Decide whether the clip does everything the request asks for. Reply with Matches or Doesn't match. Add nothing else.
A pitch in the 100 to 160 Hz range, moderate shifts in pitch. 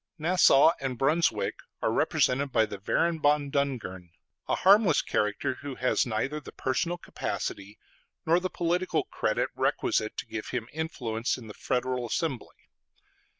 Doesn't match